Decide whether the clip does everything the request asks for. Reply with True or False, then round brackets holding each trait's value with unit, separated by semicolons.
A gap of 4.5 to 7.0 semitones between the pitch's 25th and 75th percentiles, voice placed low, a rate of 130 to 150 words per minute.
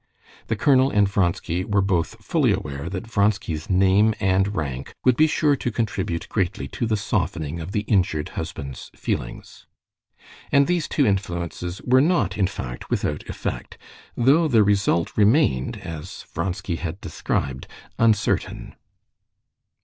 True (5.0 semitones; 95 Hz; 140 wpm)